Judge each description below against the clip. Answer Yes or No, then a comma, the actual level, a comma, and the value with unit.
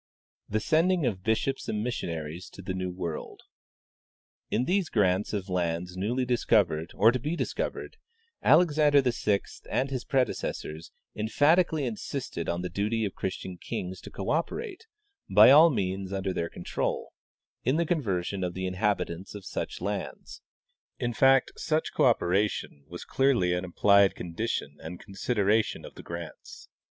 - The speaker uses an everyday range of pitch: No, wide, 6.5 semitones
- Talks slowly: No, average, 150 wpm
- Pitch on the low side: Yes, low, 105 Hz